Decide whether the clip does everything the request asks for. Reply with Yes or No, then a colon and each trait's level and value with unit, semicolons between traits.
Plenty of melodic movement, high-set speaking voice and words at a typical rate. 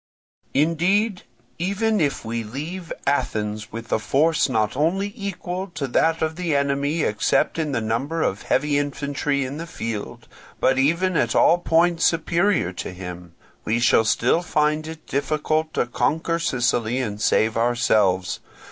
No: wide, 6.3 semitones; medium, 145 Hz; average, 150 wpm